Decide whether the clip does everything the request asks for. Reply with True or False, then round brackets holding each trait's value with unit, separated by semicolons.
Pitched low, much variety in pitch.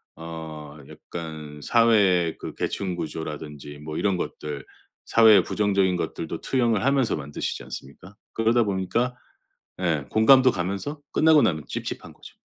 True (90 Hz; 6.5 semitones)